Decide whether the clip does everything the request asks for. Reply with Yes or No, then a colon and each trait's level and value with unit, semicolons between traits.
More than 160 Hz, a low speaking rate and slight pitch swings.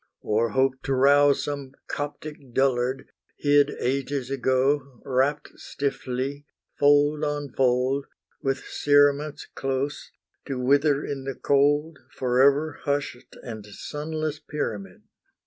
No: medium, 140 Hz; slow, 110 wpm; narrow, 1.9 semitones